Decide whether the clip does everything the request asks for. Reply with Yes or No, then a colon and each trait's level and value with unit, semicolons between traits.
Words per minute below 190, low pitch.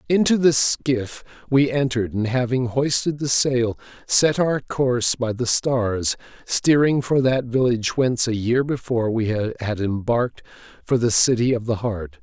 Yes: average, 160 wpm; low, 125 Hz